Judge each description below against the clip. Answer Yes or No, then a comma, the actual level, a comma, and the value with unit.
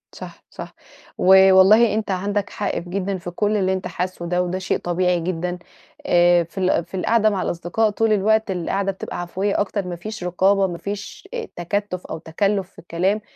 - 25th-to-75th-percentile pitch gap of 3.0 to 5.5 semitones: No, narrow, 2.4 semitones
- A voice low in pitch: No, high, 190 Hz